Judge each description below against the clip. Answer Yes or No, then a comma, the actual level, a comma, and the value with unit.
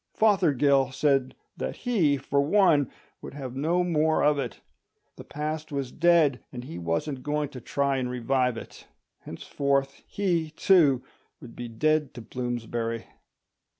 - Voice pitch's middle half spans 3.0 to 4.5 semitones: Yes, average, 3.6 semitones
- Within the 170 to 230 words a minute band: No, average, 145 wpm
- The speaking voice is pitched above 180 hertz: No, medium, 140 Hz